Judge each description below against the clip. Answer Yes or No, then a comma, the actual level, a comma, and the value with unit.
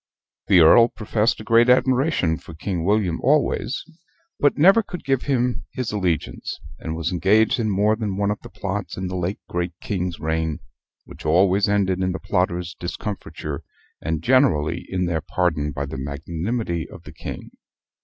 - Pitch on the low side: Yes, very low, 95 Hz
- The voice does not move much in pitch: No, average, 5.0 semitones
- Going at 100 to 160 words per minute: No, average, 170 wpm